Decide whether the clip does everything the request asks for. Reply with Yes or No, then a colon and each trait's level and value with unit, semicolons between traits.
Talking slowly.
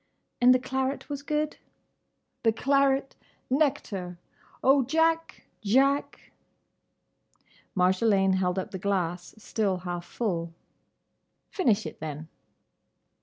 Yes: slow, 90 wpm